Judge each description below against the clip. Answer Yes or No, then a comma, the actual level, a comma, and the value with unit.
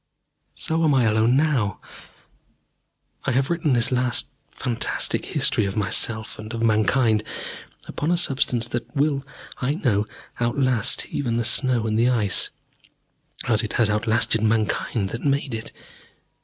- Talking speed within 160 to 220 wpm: No, average, 140 wpm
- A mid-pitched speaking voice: No, low, 120 Hz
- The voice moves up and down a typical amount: Yes, average, 3.5 semitones